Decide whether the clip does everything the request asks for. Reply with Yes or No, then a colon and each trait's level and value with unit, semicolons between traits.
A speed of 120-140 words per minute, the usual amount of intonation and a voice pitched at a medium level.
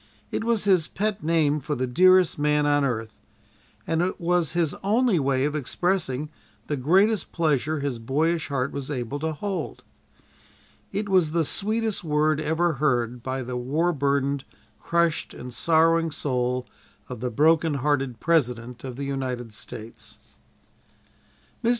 No: average, 150 wpm; average, 4.4 semitones; medium, 150 Hz